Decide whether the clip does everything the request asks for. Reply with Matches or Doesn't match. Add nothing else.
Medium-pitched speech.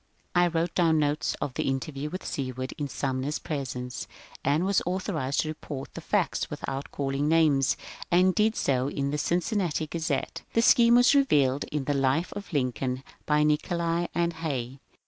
Matches